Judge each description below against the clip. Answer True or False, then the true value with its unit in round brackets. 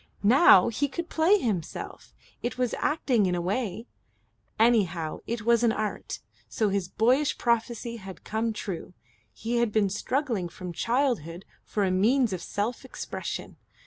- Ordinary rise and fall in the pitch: True (4.1 semitones)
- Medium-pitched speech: False (225 Hz)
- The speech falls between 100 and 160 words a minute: True (150 wpm)